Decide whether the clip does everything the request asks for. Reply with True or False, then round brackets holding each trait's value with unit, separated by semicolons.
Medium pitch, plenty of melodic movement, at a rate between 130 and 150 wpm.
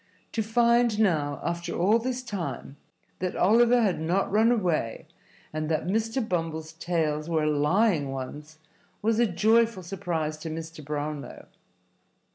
True (175 Hz; 6.1 semitones; 135 wpm)